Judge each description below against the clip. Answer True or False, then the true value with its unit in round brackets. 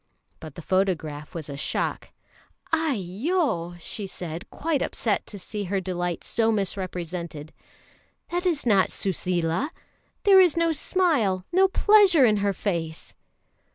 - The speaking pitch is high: True (195 Hz)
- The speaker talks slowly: True (130 wpm)